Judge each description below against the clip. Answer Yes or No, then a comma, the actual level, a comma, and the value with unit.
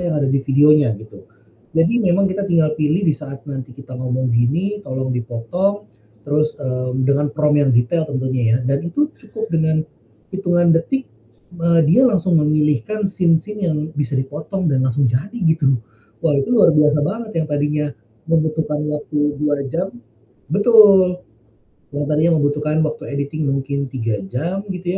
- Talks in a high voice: No, medium, 150 Hz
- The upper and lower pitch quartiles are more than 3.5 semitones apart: Yes, average, 4.4 semitones